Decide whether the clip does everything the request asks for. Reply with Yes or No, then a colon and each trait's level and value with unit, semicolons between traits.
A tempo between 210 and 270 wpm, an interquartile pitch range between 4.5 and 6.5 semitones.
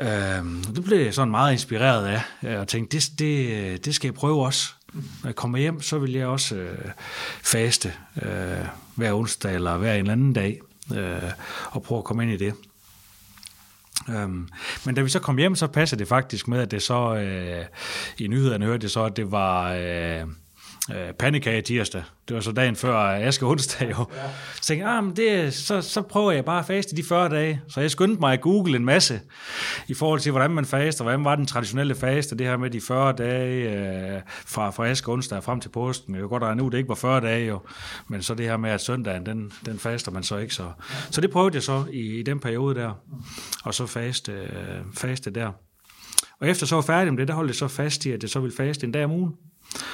Yes: fast, 225 wpm; average, 5.2 semitones